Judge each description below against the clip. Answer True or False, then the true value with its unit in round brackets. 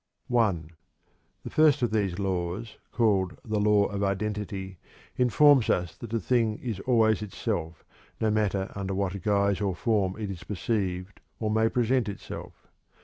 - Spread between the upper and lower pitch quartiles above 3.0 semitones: False (2.7 semitones)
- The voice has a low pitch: True (105 Hz)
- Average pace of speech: True (150 wpm)